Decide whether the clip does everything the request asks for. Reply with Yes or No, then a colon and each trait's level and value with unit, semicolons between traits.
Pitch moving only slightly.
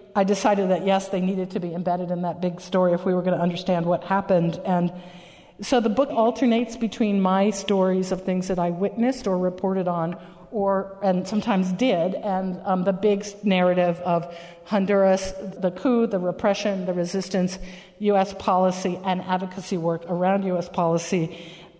Yes: narrow, 1.8 semitones